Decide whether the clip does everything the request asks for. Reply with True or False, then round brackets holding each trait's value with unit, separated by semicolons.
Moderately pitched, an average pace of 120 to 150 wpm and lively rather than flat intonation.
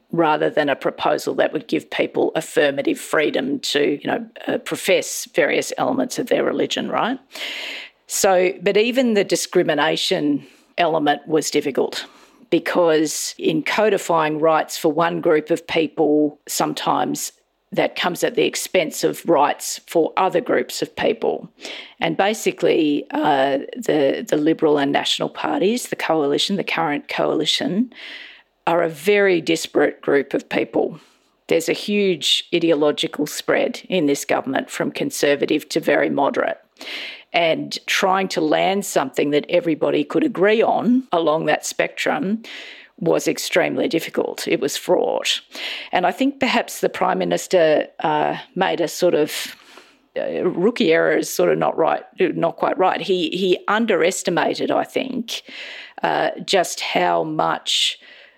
True (180 Hz; 140 wpm; 7.9 semitones)